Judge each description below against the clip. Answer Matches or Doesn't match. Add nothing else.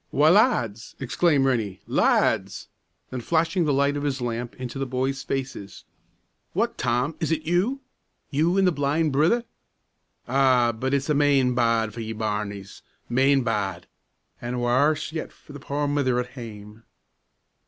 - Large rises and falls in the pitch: Doesn't match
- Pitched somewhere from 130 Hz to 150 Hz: Matches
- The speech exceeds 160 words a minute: Doesn't match